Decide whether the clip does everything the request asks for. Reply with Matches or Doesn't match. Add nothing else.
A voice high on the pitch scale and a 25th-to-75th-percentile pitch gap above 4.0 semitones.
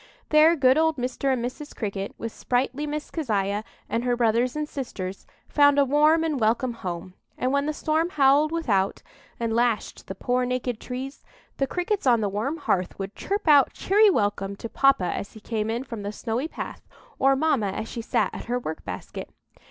Matches